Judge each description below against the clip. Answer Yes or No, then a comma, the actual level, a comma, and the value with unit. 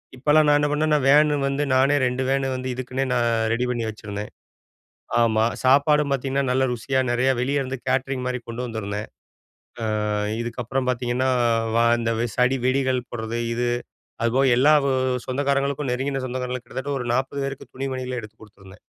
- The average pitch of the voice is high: No, low, 130 Hz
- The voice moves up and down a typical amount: No, narrow, 2.2 semitones